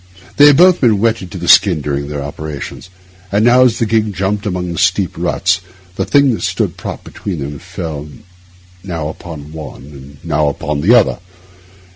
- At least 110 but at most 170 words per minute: No, average, 185 wpm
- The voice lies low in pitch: Yes, very low, 90 Hz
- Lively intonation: Yes, wide, 6.6 semitones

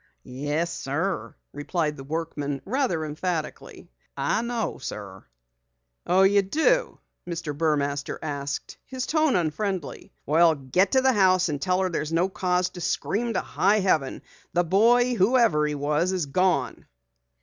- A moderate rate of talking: Yes, average, 145 wpm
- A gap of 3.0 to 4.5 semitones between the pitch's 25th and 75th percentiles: No, average, 4.9 semitones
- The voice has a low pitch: No, medium, 175 Hz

